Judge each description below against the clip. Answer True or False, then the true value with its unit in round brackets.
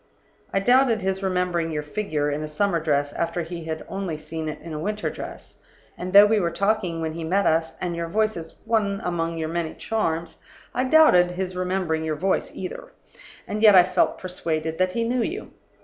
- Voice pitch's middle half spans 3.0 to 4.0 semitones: True (3.7 semitones)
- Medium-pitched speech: True (180 Hz)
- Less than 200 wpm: False (205 wpm)